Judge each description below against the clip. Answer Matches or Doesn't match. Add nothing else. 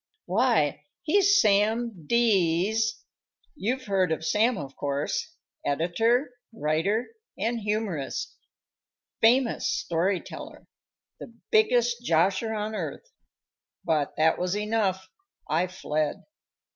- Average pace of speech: Doesn't match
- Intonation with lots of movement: Matches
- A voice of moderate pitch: Doesn't match